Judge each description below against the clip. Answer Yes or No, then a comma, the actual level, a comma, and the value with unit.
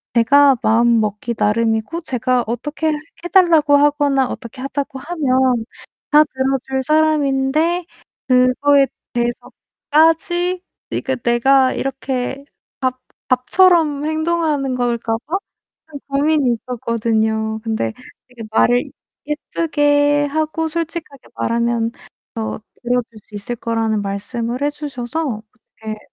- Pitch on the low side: No, very high, 265 Hz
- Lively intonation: No, average, 4.2 semitones